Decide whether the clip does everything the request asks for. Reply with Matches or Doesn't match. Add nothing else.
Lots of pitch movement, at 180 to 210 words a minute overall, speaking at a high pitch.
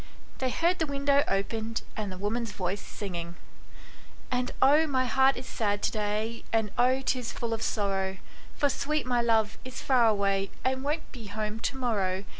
Doesn't match